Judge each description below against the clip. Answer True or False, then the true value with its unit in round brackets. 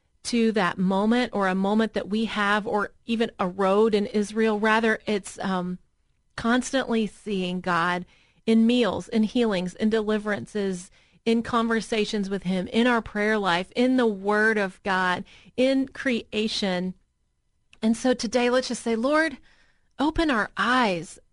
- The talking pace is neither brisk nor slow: True (145 wpm)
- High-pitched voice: True (215 Hz)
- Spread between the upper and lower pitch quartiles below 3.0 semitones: False (3.3 semitones)